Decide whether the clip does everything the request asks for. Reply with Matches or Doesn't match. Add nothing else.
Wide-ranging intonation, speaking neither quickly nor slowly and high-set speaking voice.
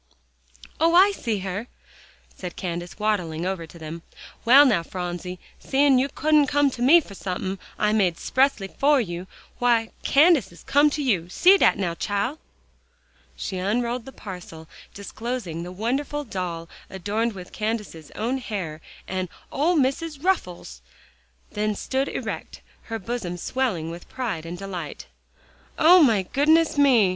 Matches